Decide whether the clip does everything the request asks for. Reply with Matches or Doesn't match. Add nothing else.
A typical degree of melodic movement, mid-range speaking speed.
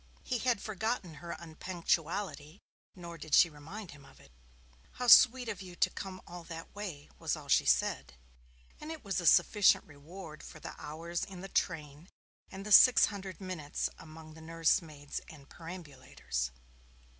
Matches